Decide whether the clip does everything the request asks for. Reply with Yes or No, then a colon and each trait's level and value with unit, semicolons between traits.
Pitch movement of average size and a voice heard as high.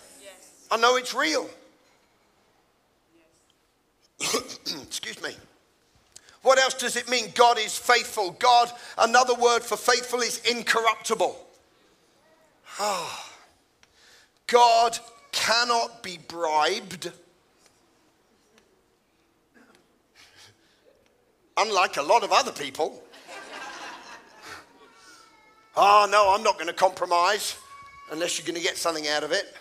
Yes: average, 4.7 semitones; high, 235 Hz